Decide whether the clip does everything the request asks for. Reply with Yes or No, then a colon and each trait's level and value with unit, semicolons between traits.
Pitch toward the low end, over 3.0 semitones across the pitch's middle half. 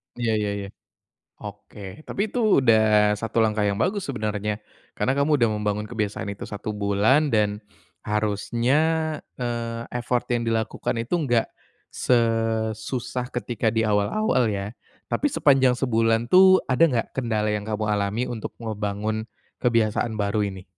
No: low, 110 Hz; average, 2.7 semitones